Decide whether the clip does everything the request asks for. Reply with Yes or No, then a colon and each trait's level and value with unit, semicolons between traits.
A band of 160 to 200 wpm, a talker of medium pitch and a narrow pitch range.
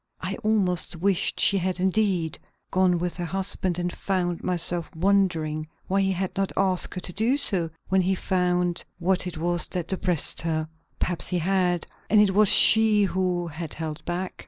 Yes: average, 180 wpm; medium, 180 Hz; narrow, 1.8 semitones